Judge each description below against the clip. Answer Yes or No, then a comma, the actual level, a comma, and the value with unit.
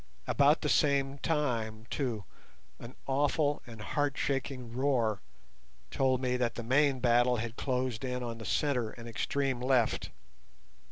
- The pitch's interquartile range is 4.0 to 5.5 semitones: No, average, 3.0 semitones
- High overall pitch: No, low, 125 Hz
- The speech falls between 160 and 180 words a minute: No, slow, 135 wpm